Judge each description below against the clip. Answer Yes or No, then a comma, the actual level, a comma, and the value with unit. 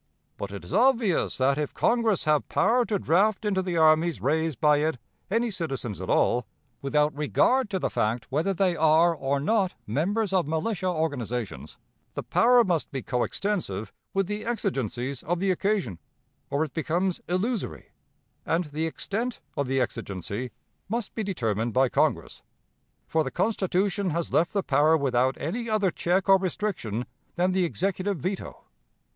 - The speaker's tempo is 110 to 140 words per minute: No, average, 160 wpm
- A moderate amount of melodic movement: No, wide, 6.2 semitones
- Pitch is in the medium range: Yes, medium, 170 Hz